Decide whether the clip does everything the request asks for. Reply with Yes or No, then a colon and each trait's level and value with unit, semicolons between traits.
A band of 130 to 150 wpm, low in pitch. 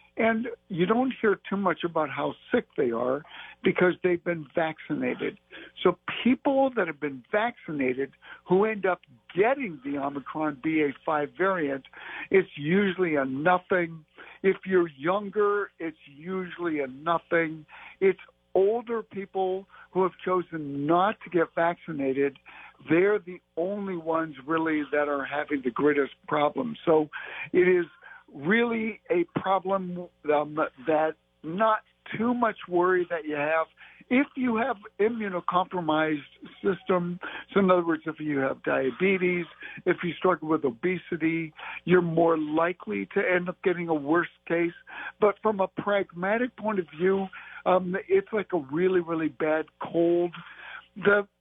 No: average, 140 wpm; medium, 175 Hz